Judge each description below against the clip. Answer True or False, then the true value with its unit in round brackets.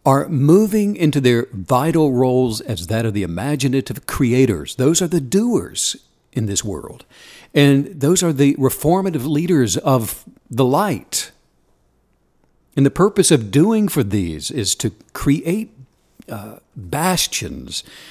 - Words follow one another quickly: False (135 wpm)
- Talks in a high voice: False (140 Hz)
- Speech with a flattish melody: False (5.2 semitones)